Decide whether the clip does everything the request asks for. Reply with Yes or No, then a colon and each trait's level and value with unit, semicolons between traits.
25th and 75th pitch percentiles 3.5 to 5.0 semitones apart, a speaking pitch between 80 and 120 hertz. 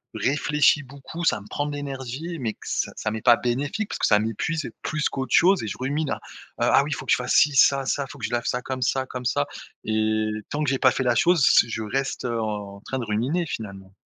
No: average, 4.5 semitones; low, 130 Hz